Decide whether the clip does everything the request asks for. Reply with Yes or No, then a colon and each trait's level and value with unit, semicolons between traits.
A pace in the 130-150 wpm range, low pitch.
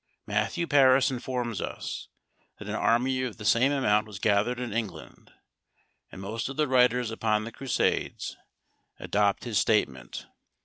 Yes: average, 145 wpm; low, 115 Hz